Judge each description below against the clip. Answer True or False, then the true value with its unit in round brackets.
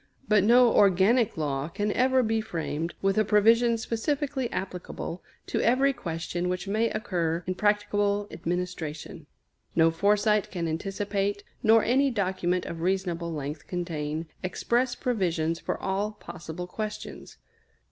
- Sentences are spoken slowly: True (130 wpm)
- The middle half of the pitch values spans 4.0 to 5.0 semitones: True (4.4 semitones)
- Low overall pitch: False (195 Hz)